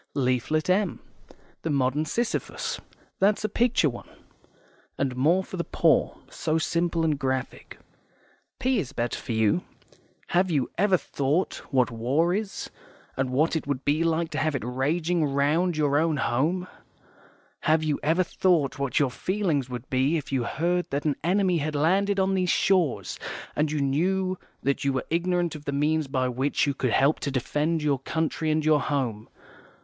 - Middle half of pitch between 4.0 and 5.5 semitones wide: Yes, average, 4.3 semitones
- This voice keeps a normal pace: Yes, average, 175 wpm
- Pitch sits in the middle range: Yes, medium, 155 Hz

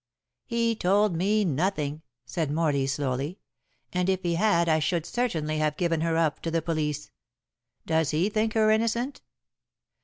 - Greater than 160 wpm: No, average, 155 wpm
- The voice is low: No, medium, 170 Hz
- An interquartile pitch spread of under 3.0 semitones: No, average, 5.1 semitones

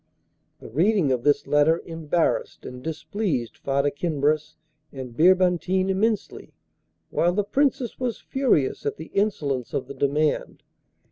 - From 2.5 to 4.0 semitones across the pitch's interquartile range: No, average, 5.3 semitones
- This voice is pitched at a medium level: Yes, medium, 160 Hz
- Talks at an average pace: No, slow, 130 wpm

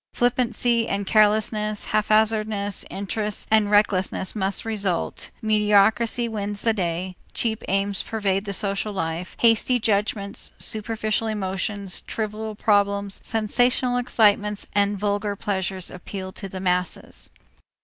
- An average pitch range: No, narrow, 1.8 semitones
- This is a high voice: Yes, high, 210 Hz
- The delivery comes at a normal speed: No, slow, 115 wpm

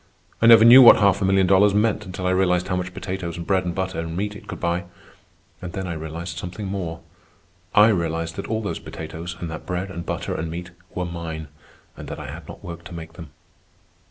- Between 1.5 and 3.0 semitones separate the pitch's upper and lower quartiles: Yes, narrow, 2.6 semitones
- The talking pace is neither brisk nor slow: No, fast, 230 wpm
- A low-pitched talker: Yes, very low, 90 Hz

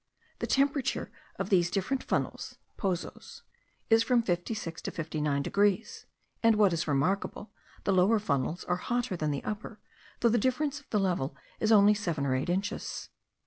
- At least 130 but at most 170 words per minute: Yes, average, 165 wpm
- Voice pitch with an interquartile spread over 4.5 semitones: Yes, average, 5.1 semitones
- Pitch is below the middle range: No, high, 200 Hz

